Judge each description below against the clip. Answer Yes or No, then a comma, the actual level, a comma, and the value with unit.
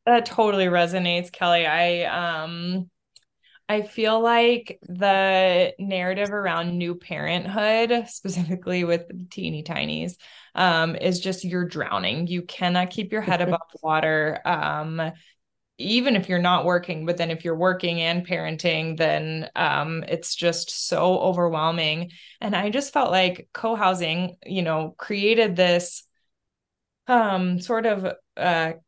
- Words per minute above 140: No, slow, 135 wpm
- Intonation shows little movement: Yes, narrow, 2.3 semitones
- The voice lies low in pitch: No, medium, 180 Hz